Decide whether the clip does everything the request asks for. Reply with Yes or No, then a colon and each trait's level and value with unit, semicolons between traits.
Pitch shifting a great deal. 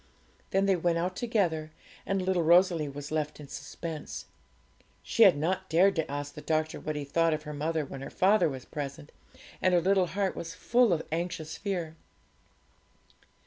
No: average, 3.5 semitones